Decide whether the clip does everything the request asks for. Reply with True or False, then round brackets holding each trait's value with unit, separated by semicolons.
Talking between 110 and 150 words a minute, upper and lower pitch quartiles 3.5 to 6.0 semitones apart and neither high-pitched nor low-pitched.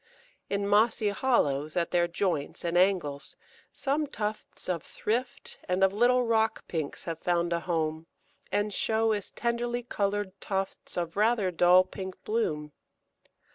False (140 wpm; 4.5 semitones; 195 Hz)